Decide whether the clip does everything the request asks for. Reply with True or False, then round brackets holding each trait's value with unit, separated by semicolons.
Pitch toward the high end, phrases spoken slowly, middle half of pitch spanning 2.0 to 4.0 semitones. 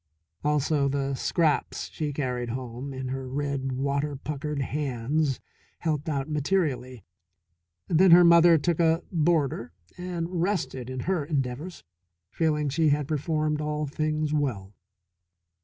False (150 Hz; 125 wpm; 3.0 semitones)